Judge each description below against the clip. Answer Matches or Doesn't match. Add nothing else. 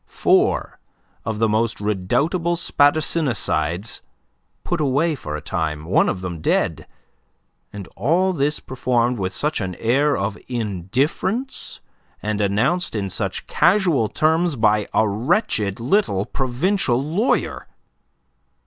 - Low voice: Matches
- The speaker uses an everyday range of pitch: Doesn't match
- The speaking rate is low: Matches